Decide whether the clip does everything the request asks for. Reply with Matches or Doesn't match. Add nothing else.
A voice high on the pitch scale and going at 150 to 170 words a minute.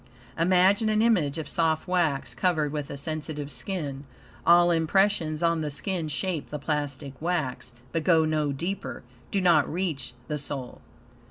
Doesn't match